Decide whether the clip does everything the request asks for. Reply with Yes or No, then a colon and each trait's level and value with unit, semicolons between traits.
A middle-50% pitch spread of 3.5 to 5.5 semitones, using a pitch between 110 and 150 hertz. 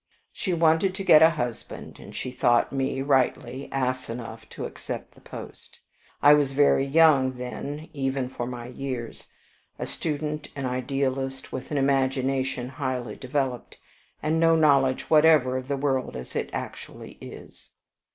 No: narrow, 2.4 semitones; low, 135 Hz